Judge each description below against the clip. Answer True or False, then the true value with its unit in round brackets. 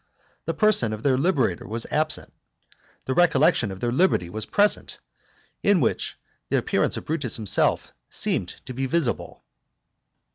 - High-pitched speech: False (130 Hz)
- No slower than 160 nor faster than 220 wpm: False (145 wpm)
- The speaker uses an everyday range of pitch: False (6.7 semitones)